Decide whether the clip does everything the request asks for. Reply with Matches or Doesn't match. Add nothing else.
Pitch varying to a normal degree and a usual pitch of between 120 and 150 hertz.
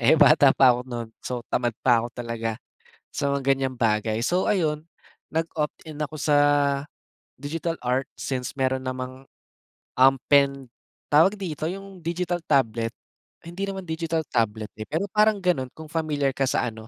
Matches